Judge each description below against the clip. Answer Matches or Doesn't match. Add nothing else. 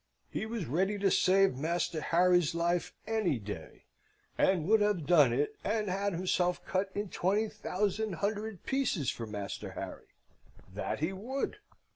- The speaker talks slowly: Doesn't match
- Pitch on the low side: Doesn't match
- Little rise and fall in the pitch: Doesn't match